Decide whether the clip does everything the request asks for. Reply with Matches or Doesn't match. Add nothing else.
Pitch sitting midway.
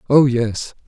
Doesn't match